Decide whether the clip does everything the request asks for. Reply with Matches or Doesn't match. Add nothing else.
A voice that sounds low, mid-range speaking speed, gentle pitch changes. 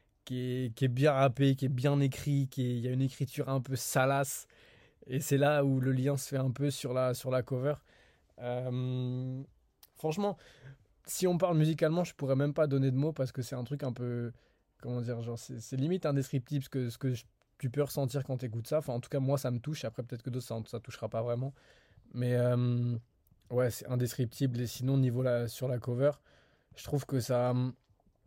Doesn't match